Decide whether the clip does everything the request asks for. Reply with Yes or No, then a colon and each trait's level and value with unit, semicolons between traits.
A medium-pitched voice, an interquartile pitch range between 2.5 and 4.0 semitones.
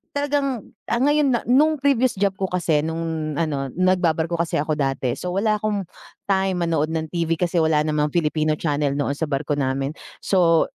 No: medium, 165 Hz; average, 4.4 semitones